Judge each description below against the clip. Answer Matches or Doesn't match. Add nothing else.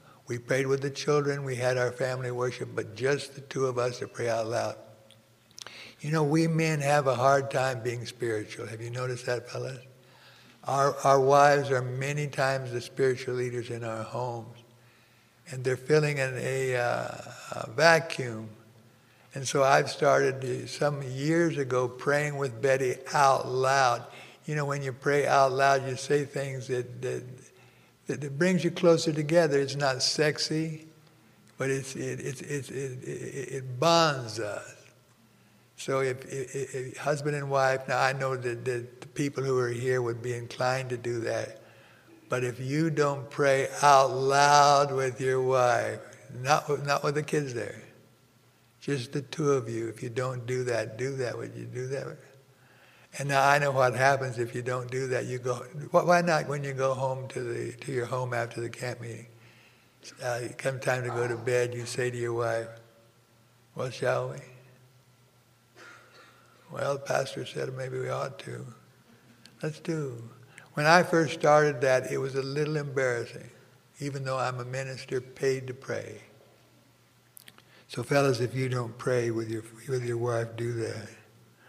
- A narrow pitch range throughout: Matches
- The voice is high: Doesn't match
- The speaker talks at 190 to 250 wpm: Doesn't match